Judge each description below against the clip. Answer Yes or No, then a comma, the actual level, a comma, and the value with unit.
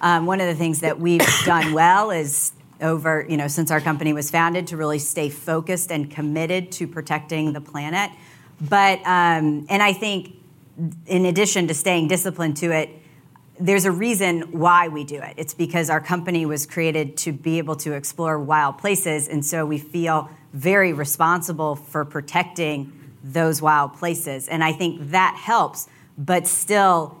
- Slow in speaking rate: No, average, 170 wpm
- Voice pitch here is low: No, medium, 160 Hz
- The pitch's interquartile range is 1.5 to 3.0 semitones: Yes, narrow, 2.6 semitones